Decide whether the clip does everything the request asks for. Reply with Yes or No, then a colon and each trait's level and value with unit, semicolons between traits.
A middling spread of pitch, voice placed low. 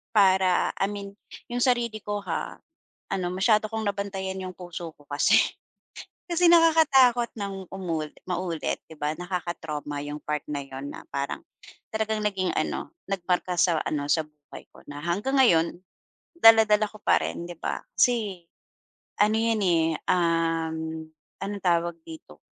No: average, 4.7 semitones; medium, 185 Hz